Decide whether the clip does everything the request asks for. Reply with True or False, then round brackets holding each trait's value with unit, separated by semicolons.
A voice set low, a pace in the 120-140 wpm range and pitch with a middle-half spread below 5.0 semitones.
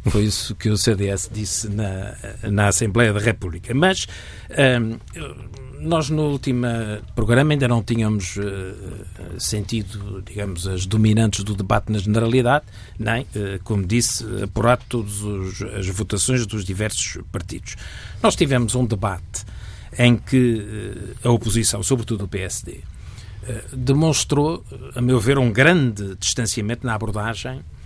True (110 Hz; 135 wpm; 3.4 semitones)